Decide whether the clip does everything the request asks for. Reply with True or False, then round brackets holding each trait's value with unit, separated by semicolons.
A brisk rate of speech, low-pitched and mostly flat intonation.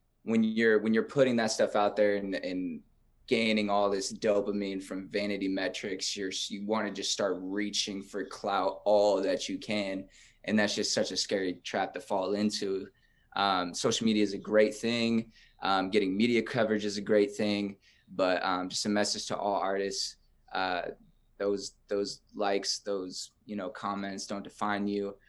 False (180 wpm; 105 Hz; 1.6 semitones)